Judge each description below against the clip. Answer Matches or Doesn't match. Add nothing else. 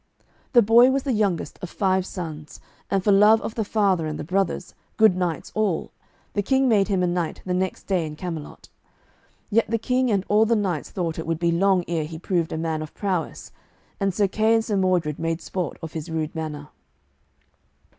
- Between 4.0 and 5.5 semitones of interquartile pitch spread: Matches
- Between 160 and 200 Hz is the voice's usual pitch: Matches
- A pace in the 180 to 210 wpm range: Matches